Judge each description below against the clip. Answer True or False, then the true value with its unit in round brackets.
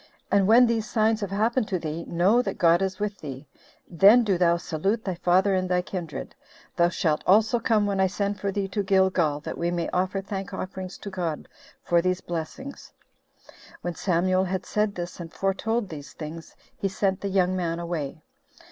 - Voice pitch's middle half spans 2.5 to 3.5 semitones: True (2.8 semitones)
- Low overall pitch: False (185 Hz)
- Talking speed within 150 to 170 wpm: False (190 wpm)